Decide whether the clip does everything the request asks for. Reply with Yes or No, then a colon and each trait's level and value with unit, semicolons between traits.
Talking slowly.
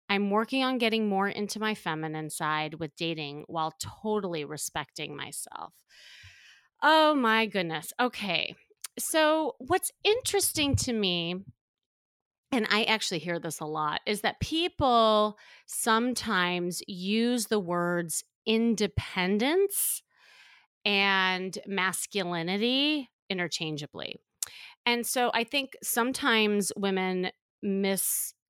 Yes: slow, 105 wpm